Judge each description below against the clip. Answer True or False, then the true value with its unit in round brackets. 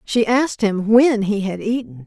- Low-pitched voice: False (215 Hz)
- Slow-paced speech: False (205 wpm)